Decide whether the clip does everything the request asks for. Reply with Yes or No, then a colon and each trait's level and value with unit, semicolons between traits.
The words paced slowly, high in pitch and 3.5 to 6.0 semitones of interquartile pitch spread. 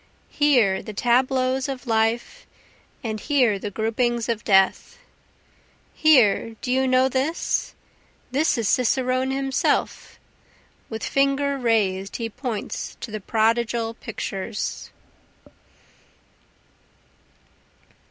No: slow, 95 wpm; high, 240 Hz; average, 3.1 semitones